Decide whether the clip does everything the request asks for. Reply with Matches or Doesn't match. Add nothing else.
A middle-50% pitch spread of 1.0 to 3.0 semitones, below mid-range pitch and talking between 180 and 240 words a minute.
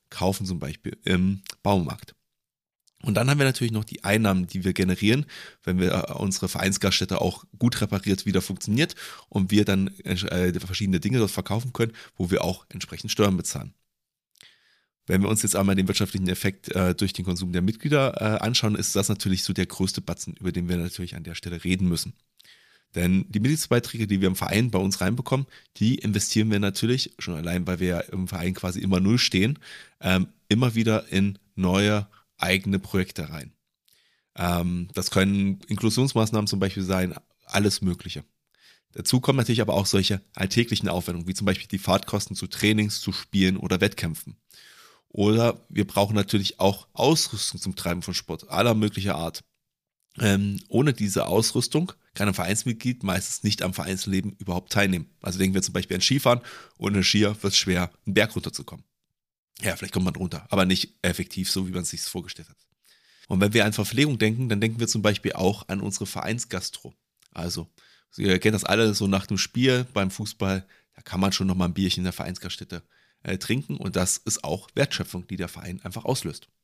Matches